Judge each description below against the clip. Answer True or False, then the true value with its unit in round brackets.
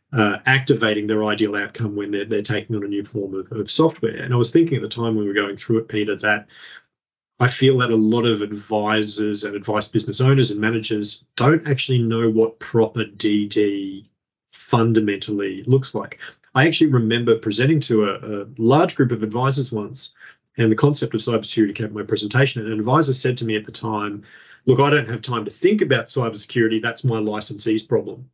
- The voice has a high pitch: False (110 Hz)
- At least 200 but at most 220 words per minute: True (205 wpm)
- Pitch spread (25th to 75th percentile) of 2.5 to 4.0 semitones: True (3.1 semitones)